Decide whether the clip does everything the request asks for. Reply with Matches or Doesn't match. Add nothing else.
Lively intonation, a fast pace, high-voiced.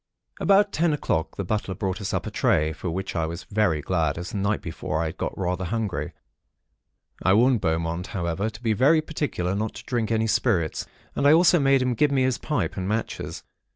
Doesn't match